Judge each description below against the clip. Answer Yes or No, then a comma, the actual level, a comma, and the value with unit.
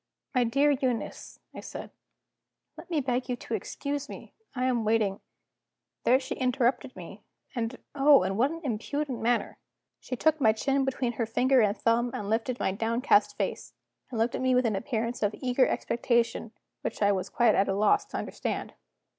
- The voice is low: No, high, 245 Hz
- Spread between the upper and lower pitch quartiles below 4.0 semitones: Yes, average, 2.9 semitones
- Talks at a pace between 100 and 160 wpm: No, average, 190 wpm